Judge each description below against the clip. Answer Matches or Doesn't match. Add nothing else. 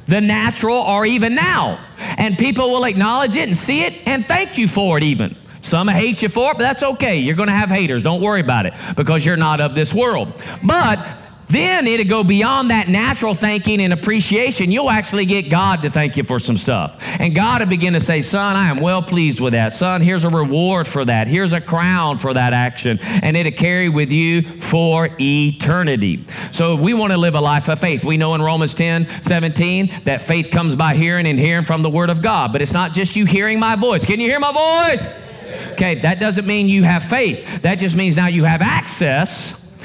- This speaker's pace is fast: Matches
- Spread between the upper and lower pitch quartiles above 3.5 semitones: Matches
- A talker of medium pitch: Matches